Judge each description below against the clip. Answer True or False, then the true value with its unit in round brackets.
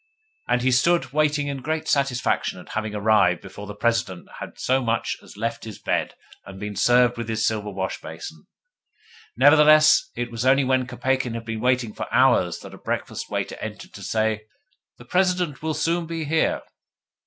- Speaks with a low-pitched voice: True (125 Hz)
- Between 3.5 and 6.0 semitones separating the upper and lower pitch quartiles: True (4.8 semitones)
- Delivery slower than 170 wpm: False (180 wpm)